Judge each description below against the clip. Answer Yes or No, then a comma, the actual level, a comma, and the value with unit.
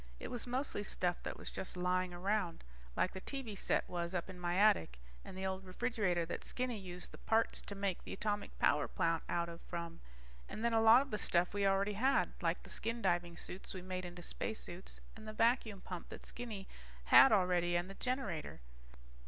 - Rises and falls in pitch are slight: No, average, 3.7 semitones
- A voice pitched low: No, high, 190 Hz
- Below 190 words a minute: No, fast, 205 wpm